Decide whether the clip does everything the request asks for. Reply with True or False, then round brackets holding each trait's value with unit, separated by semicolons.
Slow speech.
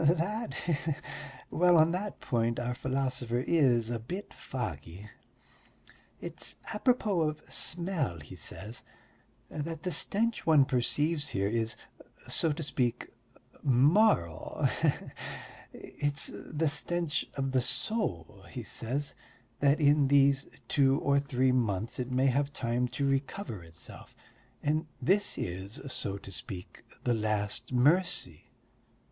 True (130 wpm)